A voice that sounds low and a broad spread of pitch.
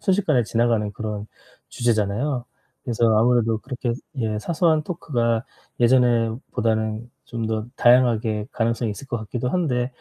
No: low, 120 Hz; narrow, 2.3 semitones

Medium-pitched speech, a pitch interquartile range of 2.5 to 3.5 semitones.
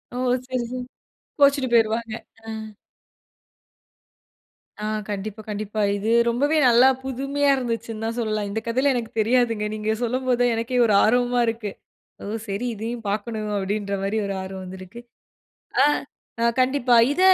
No: high, 230 Hz; average, 2.8 semitones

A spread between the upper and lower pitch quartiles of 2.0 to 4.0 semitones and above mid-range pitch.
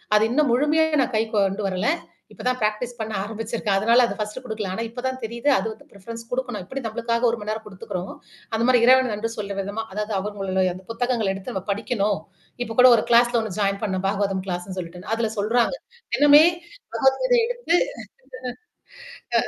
Yes: average, 3.6 semitones; high, 220 Hz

